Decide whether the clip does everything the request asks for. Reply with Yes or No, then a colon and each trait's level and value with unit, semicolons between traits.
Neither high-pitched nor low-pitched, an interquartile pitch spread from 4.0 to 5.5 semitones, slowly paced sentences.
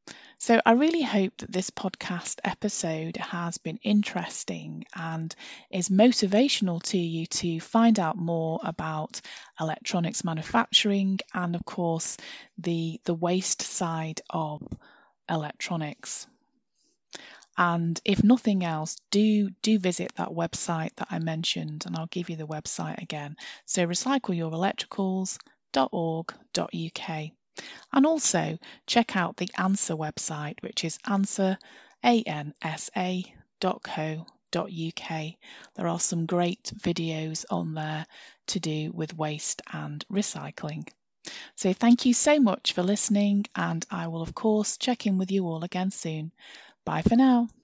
Yes: medium, 180 Hz; average, 4.3 semitones; slow, 125 wpm